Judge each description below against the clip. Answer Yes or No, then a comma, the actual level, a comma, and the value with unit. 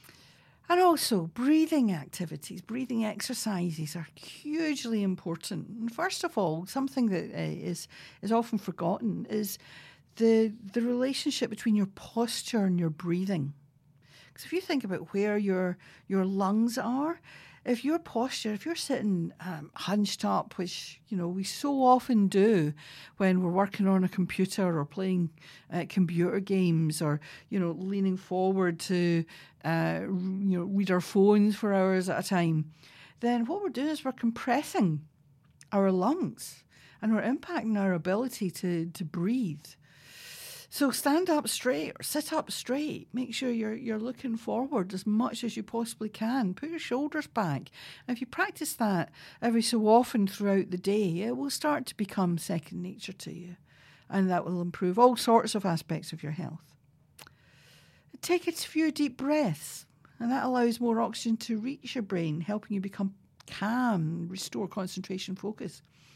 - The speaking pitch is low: No, high, 195 Hz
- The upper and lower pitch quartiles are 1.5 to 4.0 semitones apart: No, wide, 5.5 semitones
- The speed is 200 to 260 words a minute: No, average, 160 wpm